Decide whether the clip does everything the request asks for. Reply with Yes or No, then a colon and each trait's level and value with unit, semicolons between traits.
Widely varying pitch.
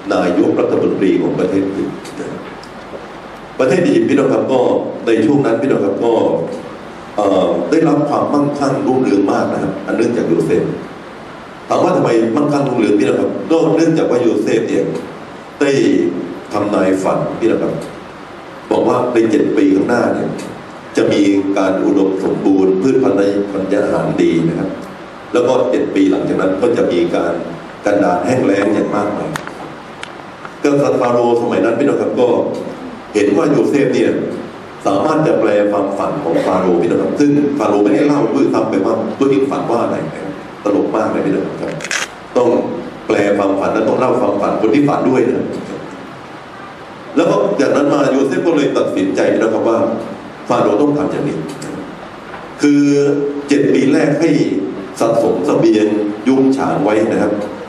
Yes: wide, 5.9 semitones